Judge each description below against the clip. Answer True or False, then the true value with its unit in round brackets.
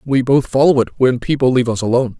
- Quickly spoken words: True (245 wpm)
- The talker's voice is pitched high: False (125 Hz)